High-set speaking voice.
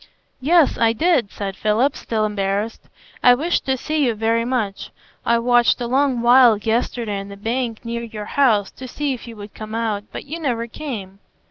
Yes: high, 235 Hz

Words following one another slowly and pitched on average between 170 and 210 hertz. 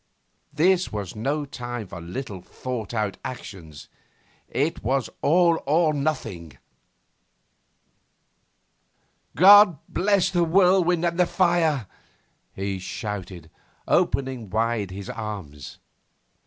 No: slow, 100 wpm; low, 125 Hz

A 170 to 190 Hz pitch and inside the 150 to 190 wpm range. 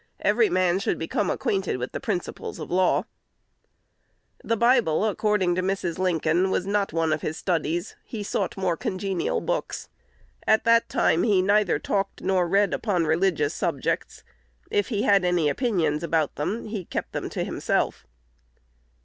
Yes: medium, 185 Hz; average, 160 wpm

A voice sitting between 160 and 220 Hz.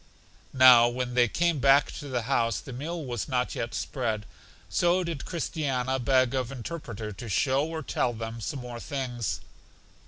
No: low, 130 Hz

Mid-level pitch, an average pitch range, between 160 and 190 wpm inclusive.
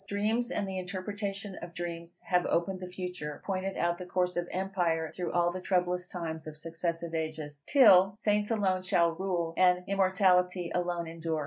No: medium, 180 Hz; narrow, 2.2 semitones; average, 175 wpm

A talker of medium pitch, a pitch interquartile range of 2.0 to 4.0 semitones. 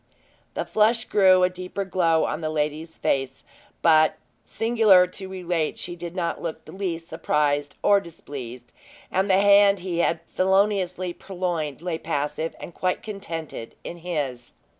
Yes: medium, 175 Hz; average, 3.4 semitones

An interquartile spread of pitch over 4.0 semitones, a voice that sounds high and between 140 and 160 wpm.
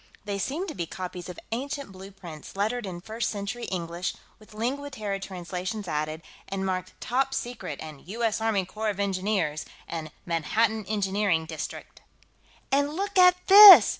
Yes: average, 4.7 semitones; high, 200 Hz; average, 155 wpm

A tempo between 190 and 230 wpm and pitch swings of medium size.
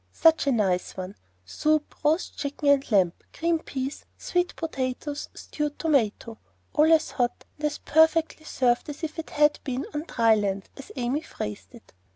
No: average, 170 wpm; average, 4.5 semitones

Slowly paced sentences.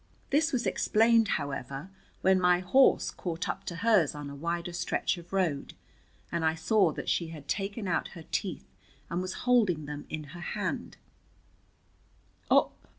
No: average, 155 wpm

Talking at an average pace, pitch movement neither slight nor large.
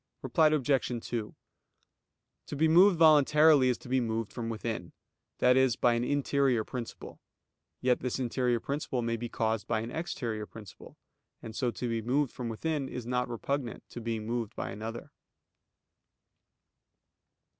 Yes: average, 155 wpm; average, 3.3 semitones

